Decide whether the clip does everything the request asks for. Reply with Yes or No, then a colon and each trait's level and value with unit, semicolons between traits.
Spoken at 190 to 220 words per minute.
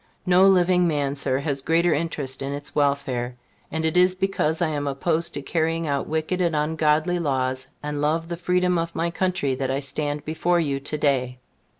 Yes: average, 195 wpm